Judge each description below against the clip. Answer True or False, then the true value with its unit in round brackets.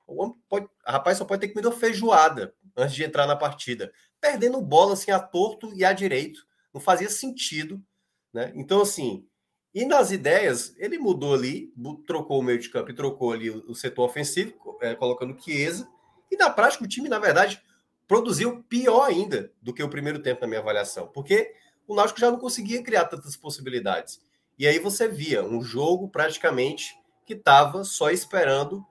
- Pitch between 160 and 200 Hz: True (190 Hz)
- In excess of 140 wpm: True (175 wpm)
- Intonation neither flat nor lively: False (7.9 semitones)